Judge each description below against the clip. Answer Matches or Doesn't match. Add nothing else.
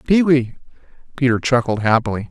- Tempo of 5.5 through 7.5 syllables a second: Matches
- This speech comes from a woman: Doesn't match